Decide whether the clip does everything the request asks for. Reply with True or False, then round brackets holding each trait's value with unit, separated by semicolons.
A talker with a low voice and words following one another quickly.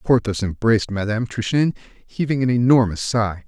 False (115 Hz; 140 wpm)